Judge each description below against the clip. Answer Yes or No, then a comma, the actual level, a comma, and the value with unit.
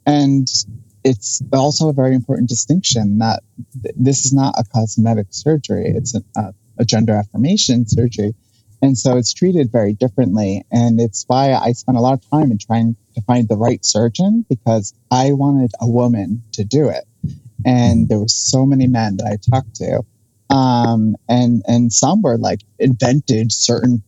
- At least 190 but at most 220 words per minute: No, average, 175 wpm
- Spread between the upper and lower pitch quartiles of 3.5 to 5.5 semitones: No, average, 2.9 semitones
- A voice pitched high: No, low, 120 Hz